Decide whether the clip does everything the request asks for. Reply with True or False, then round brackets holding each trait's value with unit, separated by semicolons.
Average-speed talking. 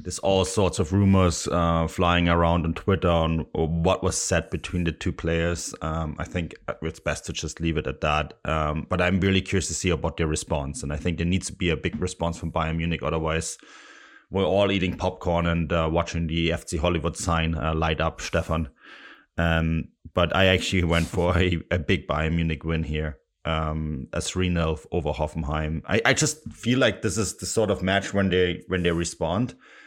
False (210 wpm)